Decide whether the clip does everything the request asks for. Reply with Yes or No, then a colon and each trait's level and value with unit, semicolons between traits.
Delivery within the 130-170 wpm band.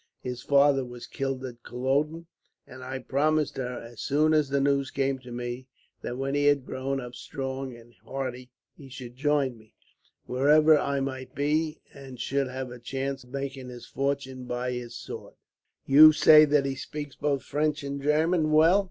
No: average, 180 wpm